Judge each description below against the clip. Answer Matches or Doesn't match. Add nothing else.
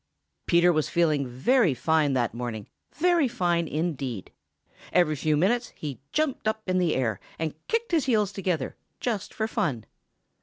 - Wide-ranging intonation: Matches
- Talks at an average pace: Matches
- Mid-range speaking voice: Matches